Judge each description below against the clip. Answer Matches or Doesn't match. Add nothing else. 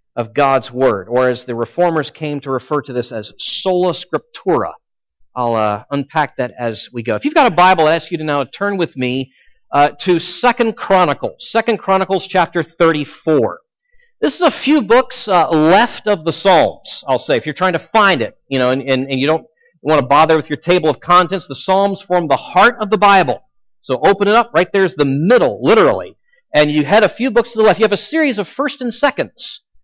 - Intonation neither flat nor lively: Doesn't match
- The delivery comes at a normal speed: Doesn't match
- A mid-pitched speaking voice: Matches